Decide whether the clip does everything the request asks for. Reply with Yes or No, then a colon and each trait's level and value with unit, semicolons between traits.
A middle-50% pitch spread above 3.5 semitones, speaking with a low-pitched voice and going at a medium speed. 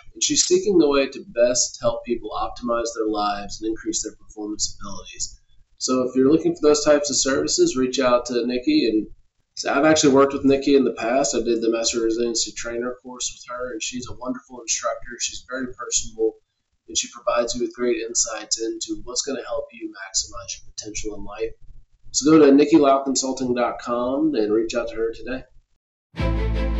Yes: average, 4.8 semitones; low, 125 Hz; average, 190 wpm